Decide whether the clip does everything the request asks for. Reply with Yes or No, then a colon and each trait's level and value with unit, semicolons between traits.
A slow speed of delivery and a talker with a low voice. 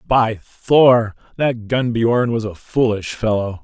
Yes: slow, 130 wpm; low, 115 Hz